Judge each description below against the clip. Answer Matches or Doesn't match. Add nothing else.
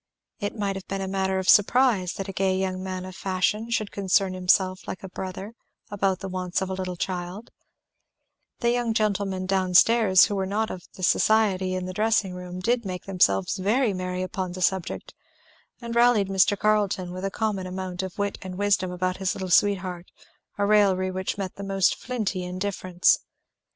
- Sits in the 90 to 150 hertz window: Doesn't match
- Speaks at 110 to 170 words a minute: Doesn't match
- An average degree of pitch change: Doesn't match